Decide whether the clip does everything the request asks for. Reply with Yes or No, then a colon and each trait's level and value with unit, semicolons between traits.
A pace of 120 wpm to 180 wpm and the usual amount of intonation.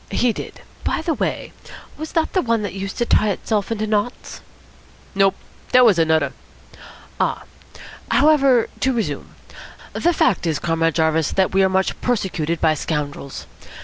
No: average, 150 wpm; wide, 6.9 semitones